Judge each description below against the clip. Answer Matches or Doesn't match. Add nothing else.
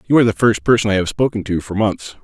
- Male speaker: Matches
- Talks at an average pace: Doesn't match